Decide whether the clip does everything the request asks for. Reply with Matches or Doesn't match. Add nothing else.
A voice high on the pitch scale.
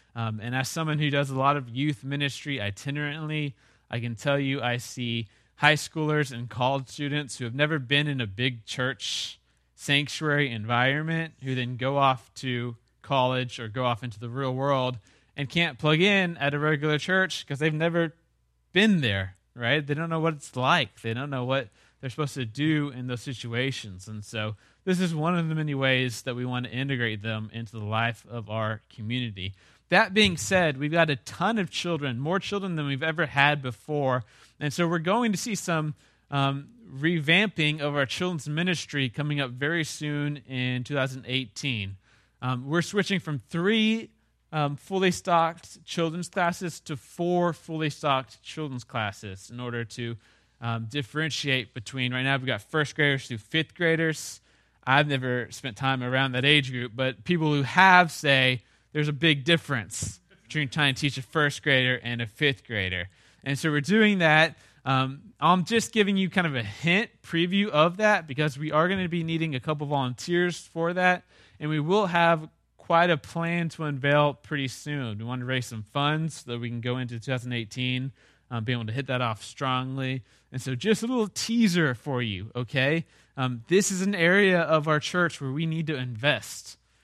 Doesn't match